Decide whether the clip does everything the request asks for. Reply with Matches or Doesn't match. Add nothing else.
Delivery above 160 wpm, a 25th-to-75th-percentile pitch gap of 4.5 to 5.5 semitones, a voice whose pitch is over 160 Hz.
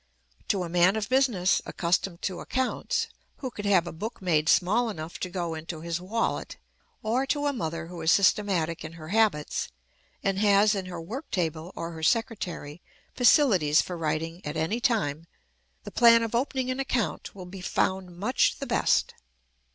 Matches